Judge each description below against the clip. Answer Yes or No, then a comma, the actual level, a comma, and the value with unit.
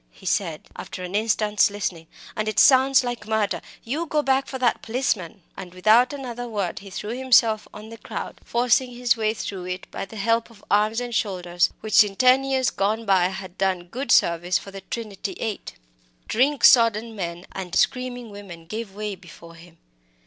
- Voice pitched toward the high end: Yes, high, 215 Hz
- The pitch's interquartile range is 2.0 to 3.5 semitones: No, average, 4.3 semitones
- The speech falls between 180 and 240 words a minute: Yes, average, 185 wpm